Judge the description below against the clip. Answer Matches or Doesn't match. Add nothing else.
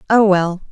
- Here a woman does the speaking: Matches